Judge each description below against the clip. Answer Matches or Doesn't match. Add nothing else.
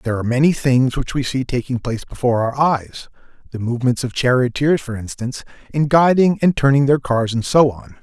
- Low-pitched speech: Matches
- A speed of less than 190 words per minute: Doesn't match